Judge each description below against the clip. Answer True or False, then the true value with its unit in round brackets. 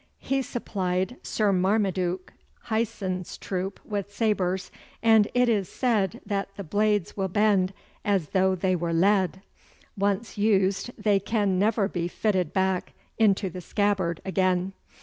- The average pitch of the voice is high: True (195 Hz)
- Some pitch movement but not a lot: False (2.2 semitones)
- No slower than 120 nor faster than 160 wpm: True (135 wpm)